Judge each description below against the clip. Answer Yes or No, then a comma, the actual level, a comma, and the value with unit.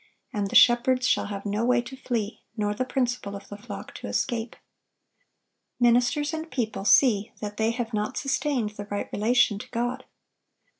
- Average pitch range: Yes, average, 3.3 semitones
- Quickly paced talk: No, average, 170 wpm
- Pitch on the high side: Yes, high, 235 Hz